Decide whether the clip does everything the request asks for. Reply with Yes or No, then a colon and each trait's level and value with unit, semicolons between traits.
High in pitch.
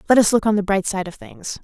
Yes: high, 205 Hz